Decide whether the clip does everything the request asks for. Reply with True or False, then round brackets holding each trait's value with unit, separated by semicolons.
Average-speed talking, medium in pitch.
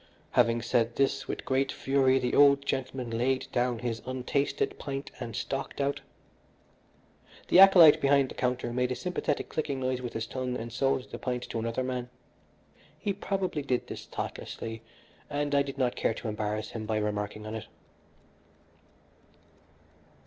False (160 wpm; 130 Hz)